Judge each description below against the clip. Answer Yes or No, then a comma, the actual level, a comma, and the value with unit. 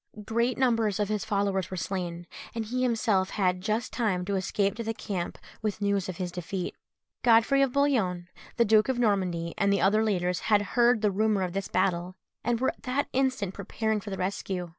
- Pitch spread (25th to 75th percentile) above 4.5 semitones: No, average, 3.5 semitones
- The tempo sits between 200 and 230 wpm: Yes, fast, 205 wpm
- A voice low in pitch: No, high, 205 Hz